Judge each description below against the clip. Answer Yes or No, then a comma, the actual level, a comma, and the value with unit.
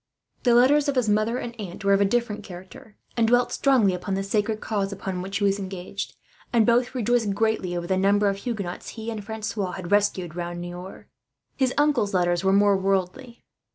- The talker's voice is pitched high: Yes, high, 205 Hz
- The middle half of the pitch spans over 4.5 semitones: No, average, 3.4 semitones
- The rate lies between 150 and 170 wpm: No, average, 200 wpm